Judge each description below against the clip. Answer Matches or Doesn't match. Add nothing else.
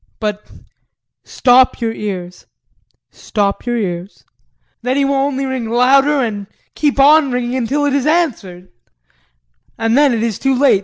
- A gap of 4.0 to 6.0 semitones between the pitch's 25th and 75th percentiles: Matches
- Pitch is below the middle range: Doesn't match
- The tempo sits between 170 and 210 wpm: Doesn't match